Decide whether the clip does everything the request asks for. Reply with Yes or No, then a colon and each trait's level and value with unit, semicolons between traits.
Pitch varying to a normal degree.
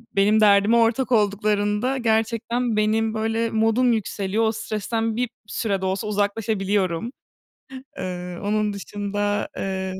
No: narrow, 2.0 semitones